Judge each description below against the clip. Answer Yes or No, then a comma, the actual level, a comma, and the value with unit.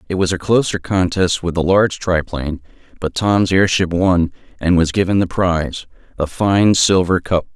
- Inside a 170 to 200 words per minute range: Yes, average, 175 wpm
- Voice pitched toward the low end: Yes, very low, 90 Hz